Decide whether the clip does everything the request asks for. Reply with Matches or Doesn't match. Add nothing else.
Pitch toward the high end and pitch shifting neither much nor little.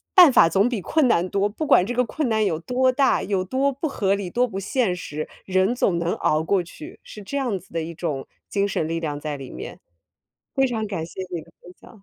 Doesn't match